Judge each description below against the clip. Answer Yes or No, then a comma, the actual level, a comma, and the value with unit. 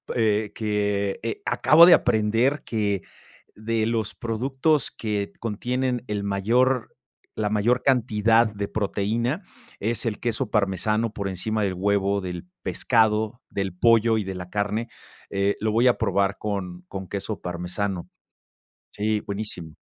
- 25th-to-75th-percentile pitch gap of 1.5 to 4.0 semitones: Yes, narrow, 2.6 semitones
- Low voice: Yes, low, 105 Hz